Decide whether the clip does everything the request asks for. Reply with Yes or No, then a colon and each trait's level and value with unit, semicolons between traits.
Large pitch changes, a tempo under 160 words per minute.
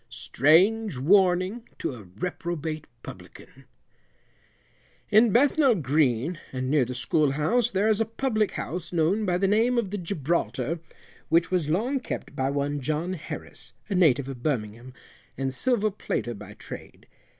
Yes: wide, 7.1 semitones; average, 150 wpm